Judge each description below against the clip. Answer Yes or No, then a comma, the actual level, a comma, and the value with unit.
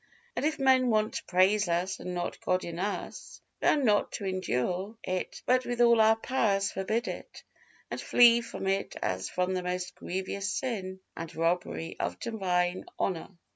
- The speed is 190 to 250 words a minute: No, average, 175 wpm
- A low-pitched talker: No, high, 190 Hz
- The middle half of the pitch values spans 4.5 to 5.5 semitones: No, average, 3.9 semitones